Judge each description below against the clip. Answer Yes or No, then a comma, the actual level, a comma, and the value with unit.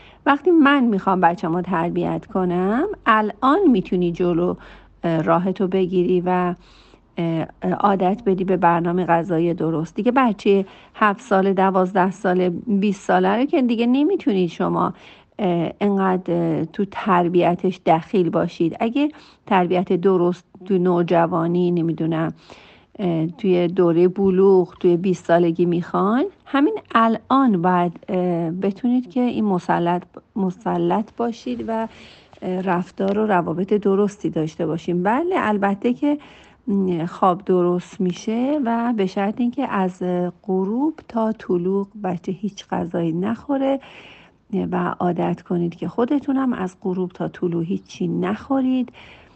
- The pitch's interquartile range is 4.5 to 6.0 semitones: No, average, 3.9 semitones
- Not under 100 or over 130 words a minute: Yes, average, 115 wpm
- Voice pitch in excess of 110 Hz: Yes, medium, 185 Hz